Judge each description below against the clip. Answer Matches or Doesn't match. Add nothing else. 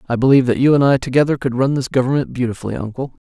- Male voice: Matches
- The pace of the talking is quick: Matches